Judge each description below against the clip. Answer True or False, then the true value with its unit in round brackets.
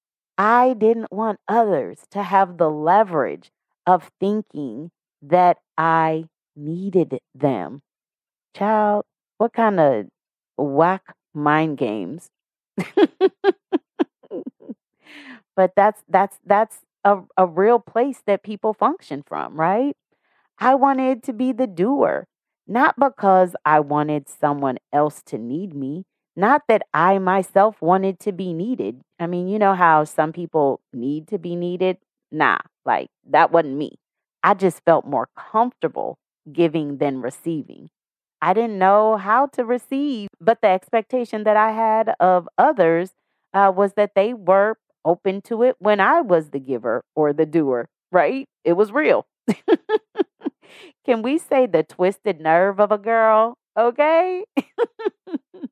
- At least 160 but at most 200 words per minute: False (135 wpm)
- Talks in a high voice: True (200 Hz)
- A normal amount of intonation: False (5.9 semitones)